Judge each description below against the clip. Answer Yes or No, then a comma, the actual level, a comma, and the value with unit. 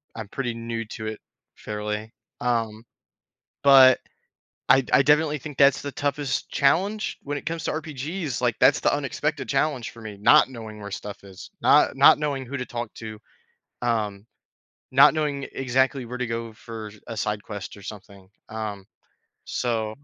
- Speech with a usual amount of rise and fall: Yes, average, 4.4 semitones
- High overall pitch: No, low, 120 Hz